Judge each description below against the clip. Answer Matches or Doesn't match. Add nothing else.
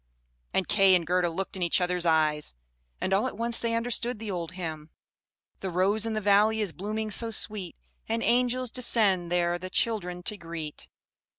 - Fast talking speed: Doesn't match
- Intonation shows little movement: Doesn't match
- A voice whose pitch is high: Matches